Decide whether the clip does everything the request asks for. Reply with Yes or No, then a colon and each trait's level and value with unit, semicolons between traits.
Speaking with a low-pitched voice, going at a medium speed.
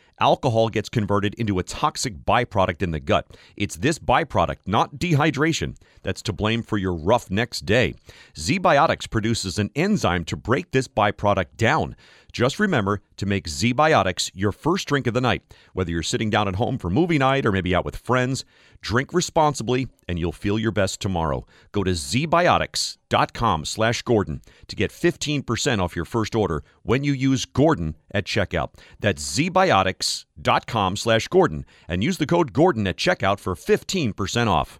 Yes: low, 110 Hz; average, 160 wpm